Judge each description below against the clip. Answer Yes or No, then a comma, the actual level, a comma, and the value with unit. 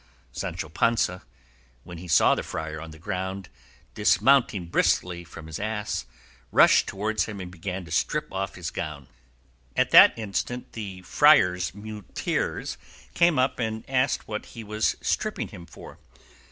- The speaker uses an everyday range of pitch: Yes, average, 4.0 semitones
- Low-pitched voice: Yes, very low, 95 Hz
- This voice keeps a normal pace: Yes, average, 150 wpm